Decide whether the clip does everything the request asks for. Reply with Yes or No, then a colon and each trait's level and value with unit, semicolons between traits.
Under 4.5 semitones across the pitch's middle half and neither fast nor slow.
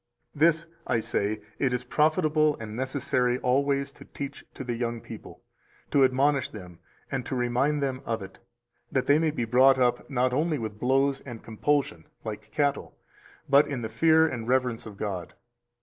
Yes: average, 3.6 semitones; average, 180 wpm